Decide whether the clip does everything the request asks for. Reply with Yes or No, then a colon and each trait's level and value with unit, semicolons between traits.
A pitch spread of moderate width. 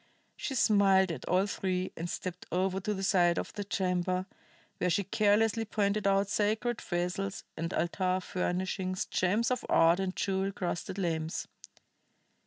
No: narrow, 2.0 semitones